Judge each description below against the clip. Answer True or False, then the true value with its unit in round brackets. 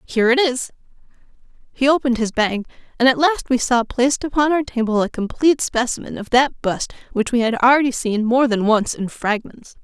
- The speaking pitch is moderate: False (245 Hz)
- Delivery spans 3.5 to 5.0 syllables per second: False (5.5 syllables/s)